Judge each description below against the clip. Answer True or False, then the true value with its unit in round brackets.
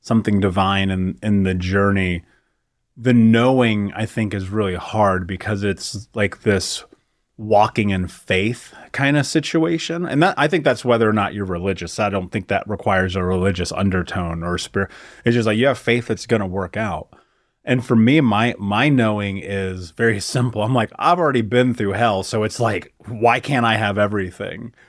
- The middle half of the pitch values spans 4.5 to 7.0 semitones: False (3.5 semitones)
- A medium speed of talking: True (190 wpm)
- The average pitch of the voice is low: True (105 Hz)